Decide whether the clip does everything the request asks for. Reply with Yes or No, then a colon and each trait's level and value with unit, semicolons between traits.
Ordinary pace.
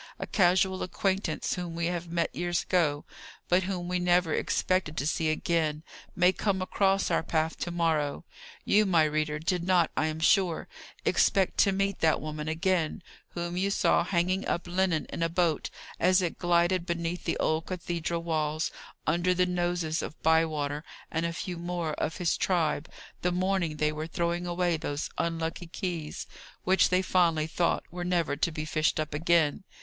Yes: average, 175 wpm